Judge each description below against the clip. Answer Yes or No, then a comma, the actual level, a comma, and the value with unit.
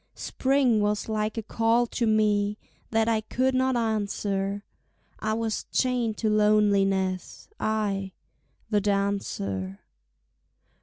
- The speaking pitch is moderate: No, high, 215 Hz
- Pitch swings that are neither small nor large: No, narrow, 2.0 semitones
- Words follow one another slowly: Yes, slow, 110 wpm